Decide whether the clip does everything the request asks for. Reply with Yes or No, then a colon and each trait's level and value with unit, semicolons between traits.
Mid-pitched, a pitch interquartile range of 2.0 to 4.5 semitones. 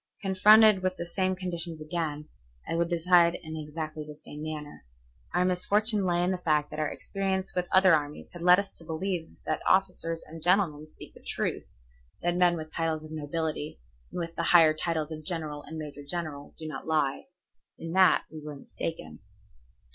Yes: medium, 165 Hz; average, 2.8 semitones